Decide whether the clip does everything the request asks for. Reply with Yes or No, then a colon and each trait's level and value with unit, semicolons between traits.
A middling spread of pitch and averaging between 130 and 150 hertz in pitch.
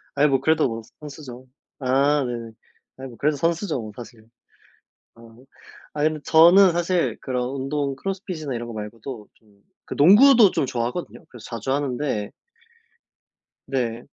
Yes: average, 4.7 semitones; low, 135 Hz